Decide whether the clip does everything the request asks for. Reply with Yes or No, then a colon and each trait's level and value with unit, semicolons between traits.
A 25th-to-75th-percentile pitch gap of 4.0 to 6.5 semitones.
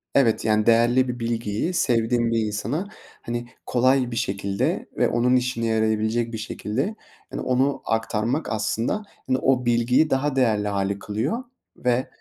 No: average, 2.7 semitones